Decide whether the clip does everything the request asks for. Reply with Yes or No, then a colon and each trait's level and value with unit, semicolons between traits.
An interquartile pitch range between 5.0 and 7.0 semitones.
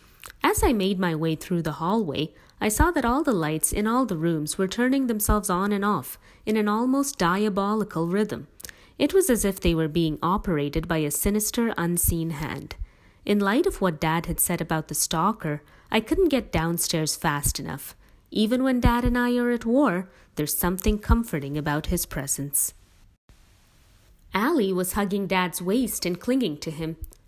Yes: wide, 5.6 semitones